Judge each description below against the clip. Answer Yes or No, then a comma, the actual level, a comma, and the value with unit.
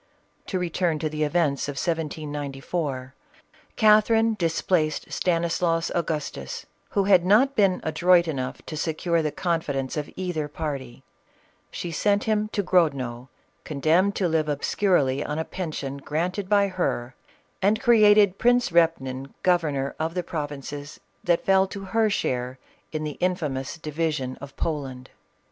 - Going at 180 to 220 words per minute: No, average, 140 wpm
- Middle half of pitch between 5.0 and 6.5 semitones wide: No, average, 4.4 semitones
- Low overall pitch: No, medium, 165 Hz